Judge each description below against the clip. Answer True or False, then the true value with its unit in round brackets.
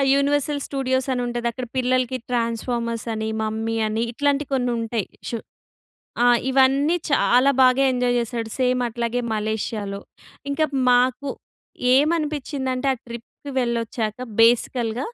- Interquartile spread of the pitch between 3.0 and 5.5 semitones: False (2.5 semitones)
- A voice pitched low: False (245 Hz)